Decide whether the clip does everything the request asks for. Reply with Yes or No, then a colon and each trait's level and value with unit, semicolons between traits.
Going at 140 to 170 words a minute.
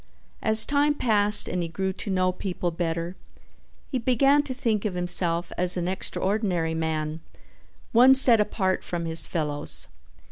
Yes: average, 150 wpm